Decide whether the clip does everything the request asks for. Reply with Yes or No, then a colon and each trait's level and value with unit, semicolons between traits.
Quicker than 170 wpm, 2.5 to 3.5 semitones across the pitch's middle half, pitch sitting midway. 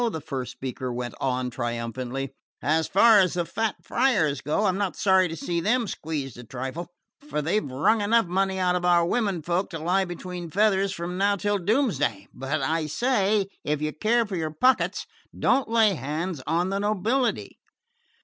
No: average, 180 wpm; wide, 5.5 semitones; medium, 175 Hz